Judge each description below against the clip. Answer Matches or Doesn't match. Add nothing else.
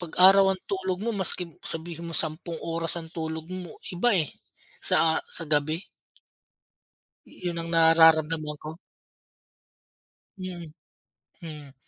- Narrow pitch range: Matches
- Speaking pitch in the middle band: Matches